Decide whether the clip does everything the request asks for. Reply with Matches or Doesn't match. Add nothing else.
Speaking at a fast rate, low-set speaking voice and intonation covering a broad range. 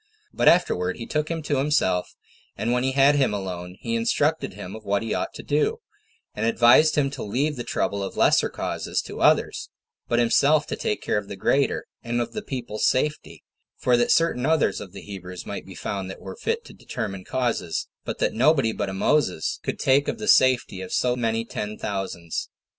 Matches